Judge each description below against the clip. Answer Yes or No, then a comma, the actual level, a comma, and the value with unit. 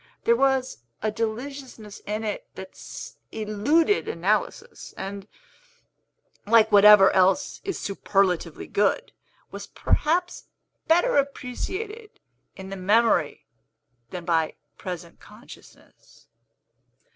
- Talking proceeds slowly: Yes, slow, 95 wpm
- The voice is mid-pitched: No, high, 215 Hz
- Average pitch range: No, wide, 6.1 semitones